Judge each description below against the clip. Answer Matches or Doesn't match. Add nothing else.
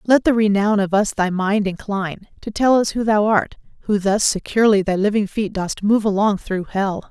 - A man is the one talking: Doesn't match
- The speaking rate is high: Matches